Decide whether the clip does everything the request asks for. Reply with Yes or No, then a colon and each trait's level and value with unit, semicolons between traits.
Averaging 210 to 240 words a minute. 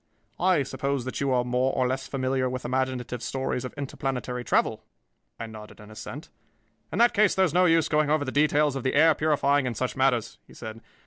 Yes: fast, 215 wpm